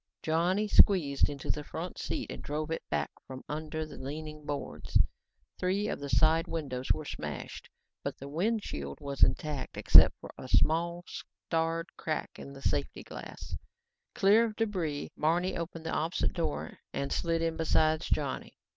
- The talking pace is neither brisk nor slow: Yes, average, 165 wpm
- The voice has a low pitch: No, medium, 160 Hz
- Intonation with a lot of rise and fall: No, average, 3.0 semitones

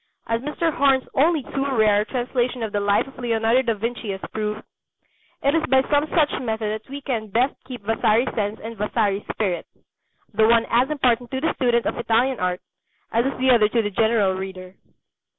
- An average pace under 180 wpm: No, average, 195 wpm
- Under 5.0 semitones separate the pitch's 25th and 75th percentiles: Yes, average, 3.6 semitones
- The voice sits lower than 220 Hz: No, high, 230 Hz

